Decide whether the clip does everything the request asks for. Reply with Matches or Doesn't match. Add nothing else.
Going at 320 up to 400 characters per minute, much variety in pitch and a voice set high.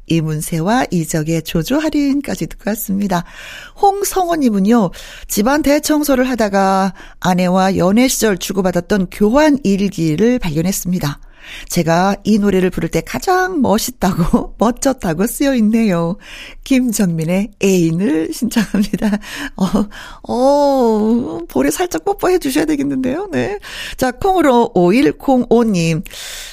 Doesn't match